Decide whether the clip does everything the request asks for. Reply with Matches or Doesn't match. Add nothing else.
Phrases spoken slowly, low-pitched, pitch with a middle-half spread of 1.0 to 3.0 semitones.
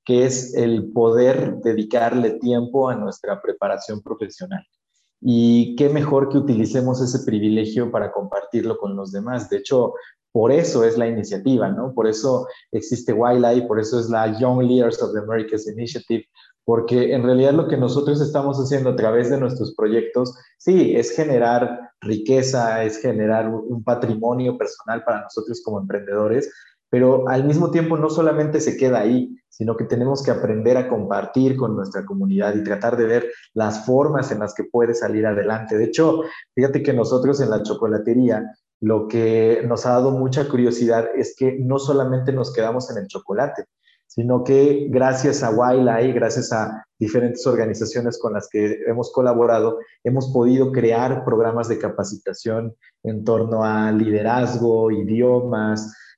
Doesn't match